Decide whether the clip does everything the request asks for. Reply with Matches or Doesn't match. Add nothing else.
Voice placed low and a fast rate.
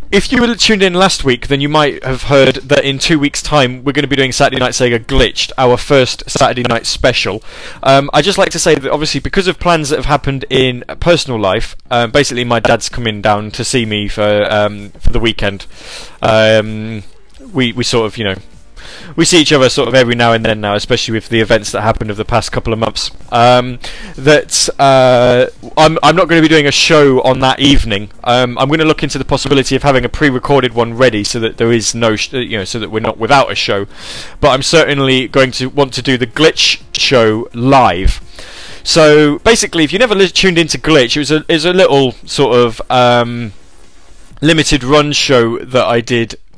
Matches